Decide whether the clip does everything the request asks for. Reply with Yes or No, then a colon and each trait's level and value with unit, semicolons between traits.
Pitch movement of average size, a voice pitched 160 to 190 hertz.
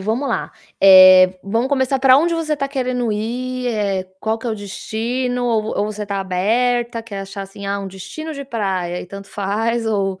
No: average, 4.1 semitones; high, 220 Hz